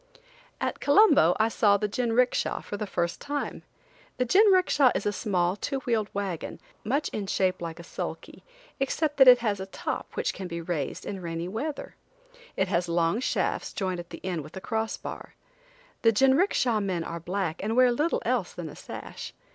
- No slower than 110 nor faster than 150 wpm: No, average, 185 wpm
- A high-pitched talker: Yes, high, 205 Hz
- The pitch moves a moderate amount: No, wide, 6.1 semitones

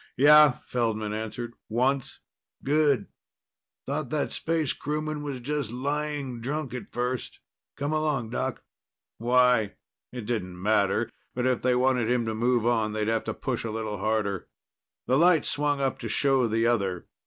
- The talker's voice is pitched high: No, low, 125 Hz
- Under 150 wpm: No, average, 155 wpm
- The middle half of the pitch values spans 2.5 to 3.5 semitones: No, average, 4.3 semitones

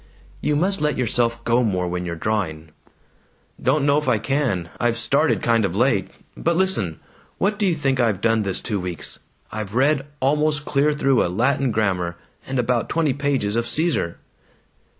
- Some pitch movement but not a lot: No, wide, 6.3 semitones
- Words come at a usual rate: Yes, average, 175 wpm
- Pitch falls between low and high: No, low, 120 Hz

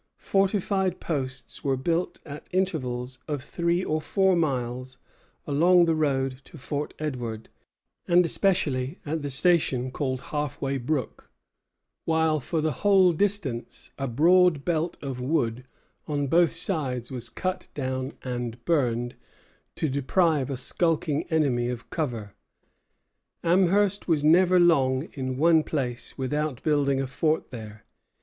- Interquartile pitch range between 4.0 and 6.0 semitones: Yes, average, 4.6 semitones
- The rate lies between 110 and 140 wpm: Yes, slow, 135 wpm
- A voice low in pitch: No, medium, 145 Hz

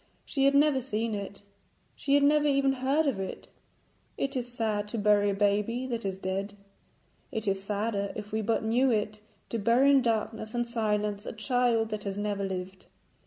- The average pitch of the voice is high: Yes, high, 220 Hz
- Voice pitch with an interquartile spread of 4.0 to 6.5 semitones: No, average, 3.6 semitones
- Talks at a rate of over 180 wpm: Yes, average, 190 wpm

